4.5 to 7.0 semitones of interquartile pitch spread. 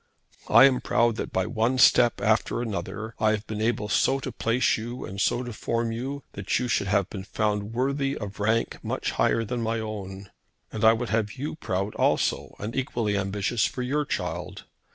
No: average, 2.9 semitones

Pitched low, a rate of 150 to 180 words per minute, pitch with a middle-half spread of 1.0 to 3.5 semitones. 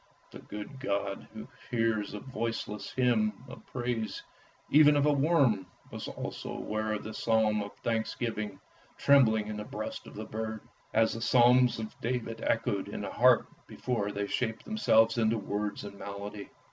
Yes: low, 110 Hz; average, 165 wpm; average, 2.7 semitones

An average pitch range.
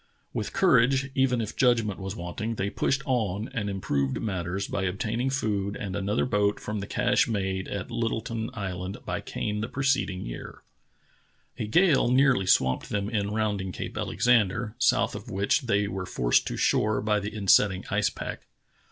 Yes: average, 3.5 semitones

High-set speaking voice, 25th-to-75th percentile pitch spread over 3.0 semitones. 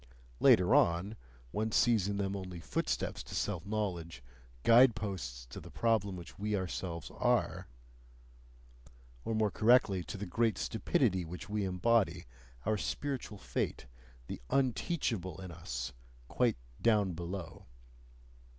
No: low, 100 Hz; average, 4.1 semitones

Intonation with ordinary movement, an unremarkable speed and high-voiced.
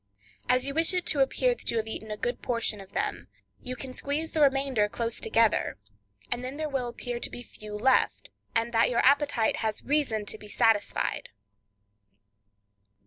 Yes: average, 3.9 semitones; average, 185 wpm; high, 245 Hz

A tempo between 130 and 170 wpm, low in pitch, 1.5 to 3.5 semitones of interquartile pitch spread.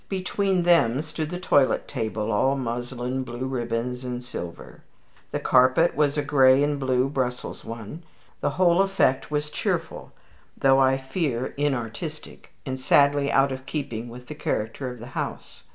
Yes: average, 155 wpm; low, 130 Hz; average, 3.1 semitones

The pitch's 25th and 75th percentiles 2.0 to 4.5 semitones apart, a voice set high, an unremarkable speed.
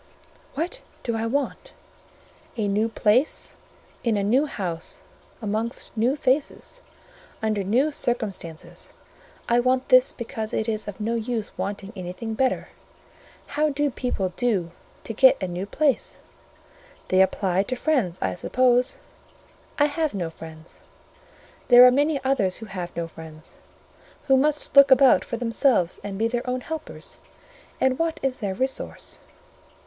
No: average, 5.0 semitones; high, 235 Hz; average, 145 wpm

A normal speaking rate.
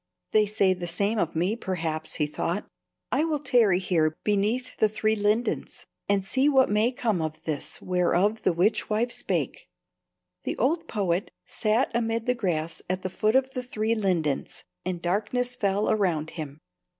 Yes: average, 170 wpm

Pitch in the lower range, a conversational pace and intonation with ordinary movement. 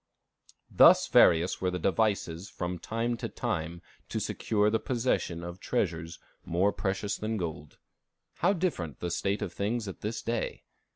Yes: very low, 95 Hz; average, 155 wpm; average, 4.4 semitones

